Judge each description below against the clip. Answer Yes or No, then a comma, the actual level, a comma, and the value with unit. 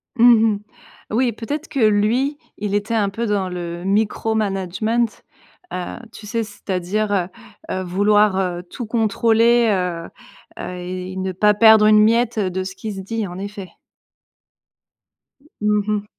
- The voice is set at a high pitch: Yes, high, 210 Hz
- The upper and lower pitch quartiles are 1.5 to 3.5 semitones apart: Yes, average, 2.9 semitones